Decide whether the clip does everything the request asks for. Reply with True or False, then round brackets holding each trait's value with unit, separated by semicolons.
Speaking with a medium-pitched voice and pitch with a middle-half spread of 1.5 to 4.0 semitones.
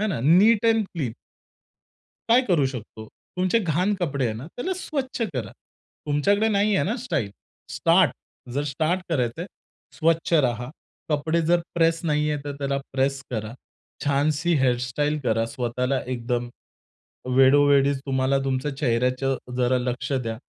False (145 Hz; 5.2 semitones)